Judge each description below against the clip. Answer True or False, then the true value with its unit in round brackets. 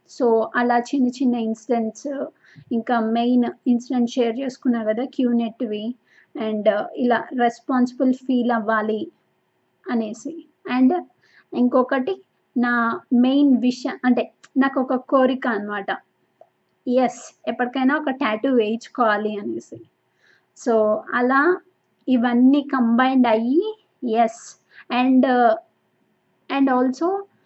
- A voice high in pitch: True (250 Hz)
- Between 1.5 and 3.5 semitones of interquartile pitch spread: True (2.5 semitones)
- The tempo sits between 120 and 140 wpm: False (95 wpm)